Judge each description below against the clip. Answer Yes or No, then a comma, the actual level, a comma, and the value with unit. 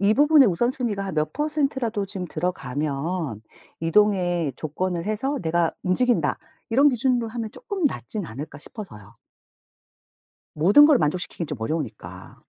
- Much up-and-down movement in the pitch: Yes, wide, 7.7 semitones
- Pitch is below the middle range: No, high, 190 Hz